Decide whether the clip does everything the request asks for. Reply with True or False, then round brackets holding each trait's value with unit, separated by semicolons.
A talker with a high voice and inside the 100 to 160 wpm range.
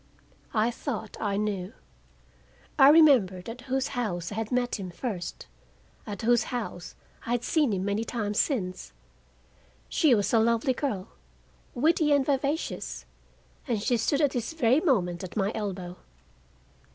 True (230 Hz; 150 wpm)